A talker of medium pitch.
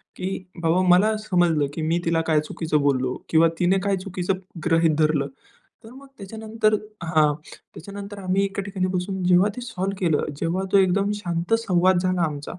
Yes: medium, 180 Hz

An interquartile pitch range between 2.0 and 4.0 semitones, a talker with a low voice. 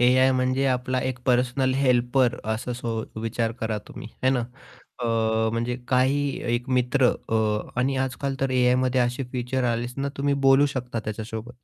No: narrow, 1.6 semitones; low, 125 Hz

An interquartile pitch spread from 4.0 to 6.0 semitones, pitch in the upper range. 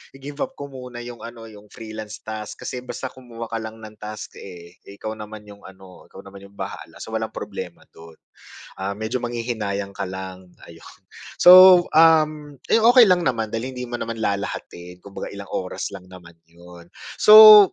No: average, 4.6 semitones; low, 110 Hz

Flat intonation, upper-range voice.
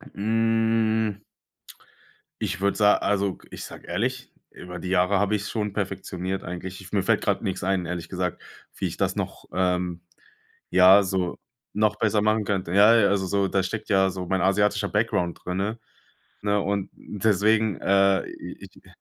No: narrow, 2.2 semitones; low, 100 Hz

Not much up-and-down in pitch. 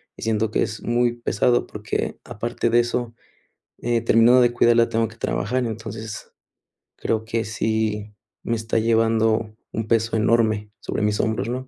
Yes: narrow, 1.3 semitones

